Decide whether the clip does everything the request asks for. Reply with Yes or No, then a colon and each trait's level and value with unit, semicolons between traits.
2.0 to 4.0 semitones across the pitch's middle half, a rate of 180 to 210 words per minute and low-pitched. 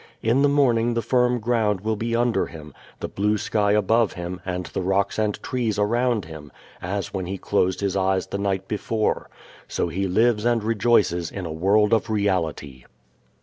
Yes: average, 3.5 semitones; average, 185 wpm; low, 105 Hz